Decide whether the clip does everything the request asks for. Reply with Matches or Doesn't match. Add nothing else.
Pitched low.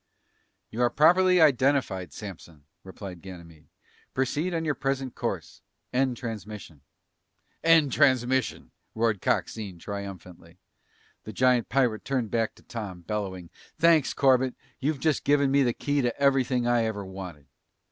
Matches